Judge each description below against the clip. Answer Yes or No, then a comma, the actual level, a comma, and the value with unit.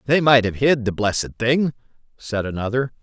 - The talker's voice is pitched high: No, low, 120 Hz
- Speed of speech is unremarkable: Yes, average, 180 wpm